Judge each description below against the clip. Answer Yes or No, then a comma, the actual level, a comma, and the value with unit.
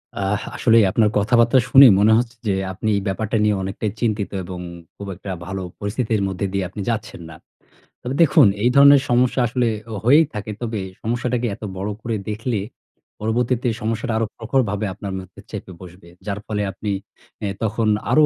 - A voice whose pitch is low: Yes, low, 110 Hz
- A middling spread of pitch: Yes, average, 3.0 semitones